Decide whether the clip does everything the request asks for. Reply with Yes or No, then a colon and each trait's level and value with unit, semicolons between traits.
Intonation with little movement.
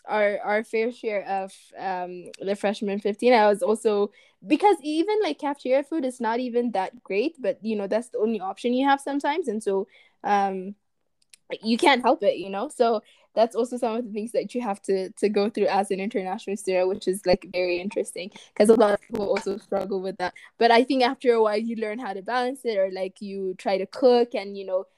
No: average, 3.7 semitones